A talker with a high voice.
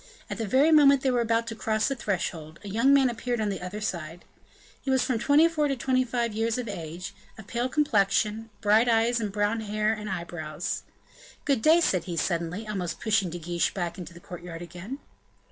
Yes: high, 215 Hz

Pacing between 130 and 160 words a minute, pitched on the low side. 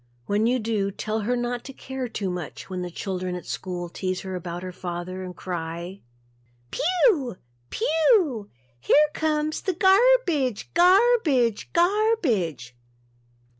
No: average, 145 wpm; high, 225 Hz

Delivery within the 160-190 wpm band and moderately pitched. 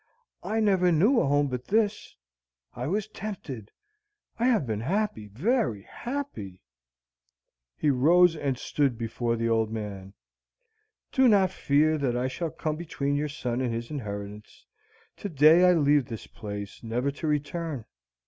No: average, 150 wpm; medium, 145 Hz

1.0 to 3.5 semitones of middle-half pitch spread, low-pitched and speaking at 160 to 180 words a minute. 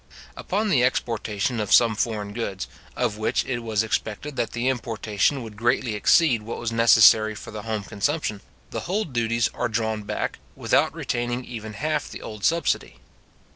Yes: narrow, 2.6 semitones; low, 115 Hz; average, 170 wpm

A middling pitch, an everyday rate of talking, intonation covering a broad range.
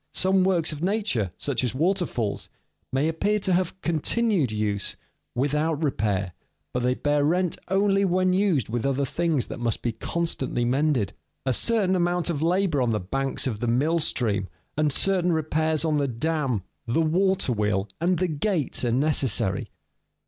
Yes: medium, 150 Hz; average, 170 wpm; wide, 6.4 semitones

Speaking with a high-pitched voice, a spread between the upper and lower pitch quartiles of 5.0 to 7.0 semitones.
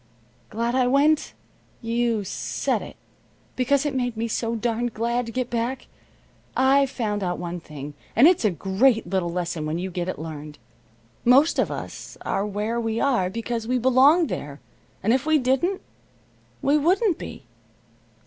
Yes: high, 235 Hz; wide, 5.5 semitones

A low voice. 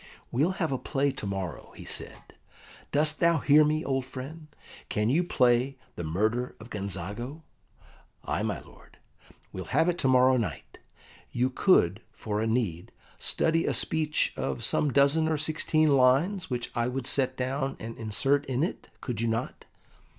Yes: low, 130 Hz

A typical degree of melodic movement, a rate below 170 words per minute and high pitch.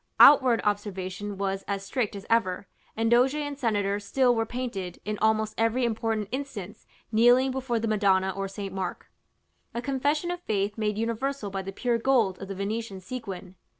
No: average, 3.8 semitones; average, 175 wpm; high, 220 Hz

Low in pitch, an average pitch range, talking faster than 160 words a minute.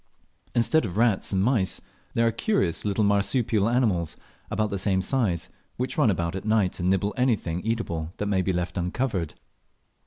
Yes: low, 100 Hz; average, 4.0 semitones; average, 175 wpm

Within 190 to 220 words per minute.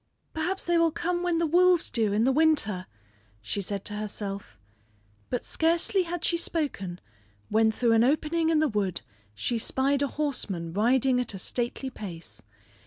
No: average, 170 wpm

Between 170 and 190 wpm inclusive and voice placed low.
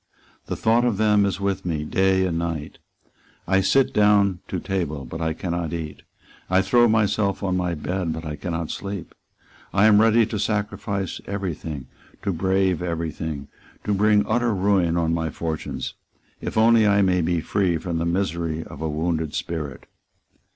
Yes: average, 175 wpm; very low, 90 Hz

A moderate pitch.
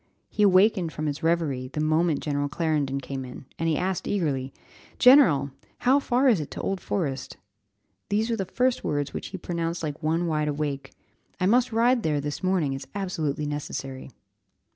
Yes: medium, 160 Hz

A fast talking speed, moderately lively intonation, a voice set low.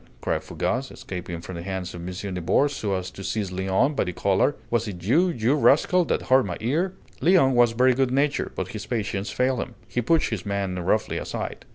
No: fast, 215 wpm; wide, 6.0 semitones; low, 110 Hz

